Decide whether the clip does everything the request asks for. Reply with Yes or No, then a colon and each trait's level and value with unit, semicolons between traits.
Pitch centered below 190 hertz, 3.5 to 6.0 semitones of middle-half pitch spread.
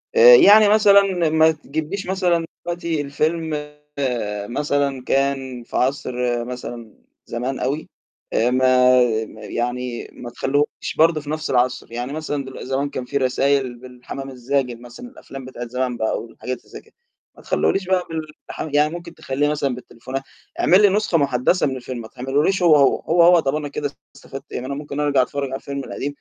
Yes: medium, 140 Hz; average, 3.8 semitones